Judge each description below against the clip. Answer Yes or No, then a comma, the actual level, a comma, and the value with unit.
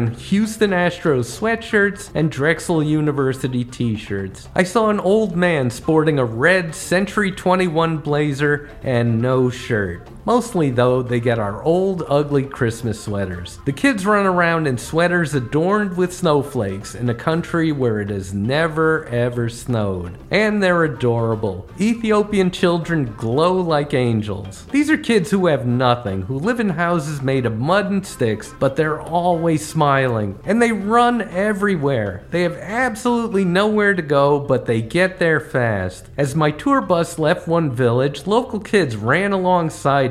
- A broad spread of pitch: Yes, wide, 7.2 semitones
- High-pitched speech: No, medium, 155 Hz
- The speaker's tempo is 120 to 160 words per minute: Yes, average, 155 wpm